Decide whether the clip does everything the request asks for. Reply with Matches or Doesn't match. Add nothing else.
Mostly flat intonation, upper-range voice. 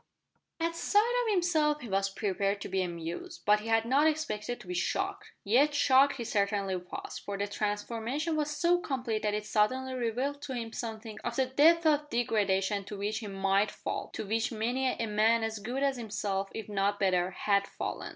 Doesn't match